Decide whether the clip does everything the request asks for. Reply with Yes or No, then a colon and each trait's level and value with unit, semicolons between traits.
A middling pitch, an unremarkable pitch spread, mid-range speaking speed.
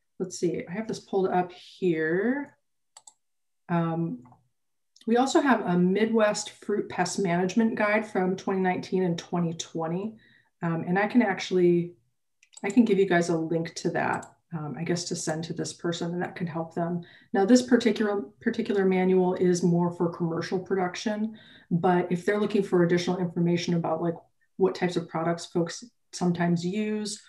Yes: medium, 180 Hz; average, 3.3 semitones; average, 165 wpm